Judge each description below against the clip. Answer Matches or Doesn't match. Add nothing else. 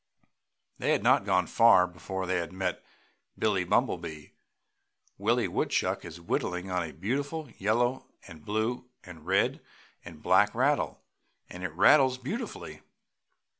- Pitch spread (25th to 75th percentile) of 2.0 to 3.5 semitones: Doesn't match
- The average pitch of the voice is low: Matches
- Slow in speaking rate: Matches